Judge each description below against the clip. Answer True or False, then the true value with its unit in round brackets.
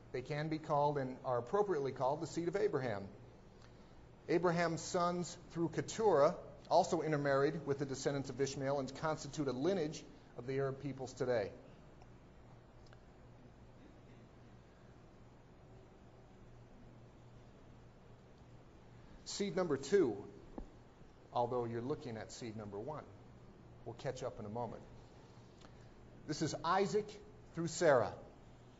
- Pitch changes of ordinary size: True (4.4 semitones)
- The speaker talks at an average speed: False (110 wpm)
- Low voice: False (145 Hz)